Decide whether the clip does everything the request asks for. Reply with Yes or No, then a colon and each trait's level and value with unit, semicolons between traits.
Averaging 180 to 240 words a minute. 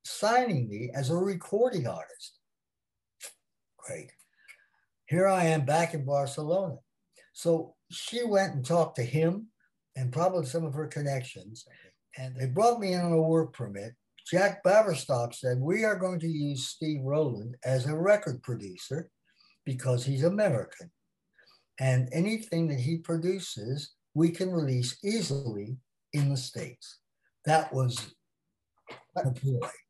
No: slow, 135 wpm